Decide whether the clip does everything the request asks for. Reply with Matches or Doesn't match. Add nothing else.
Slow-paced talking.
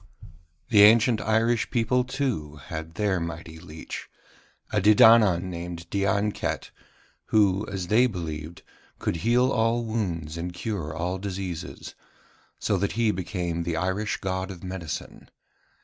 Matches